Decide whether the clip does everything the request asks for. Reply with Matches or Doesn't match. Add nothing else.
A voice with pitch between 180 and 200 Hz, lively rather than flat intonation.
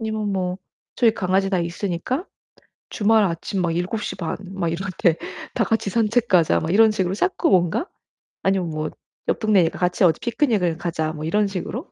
Doesn't match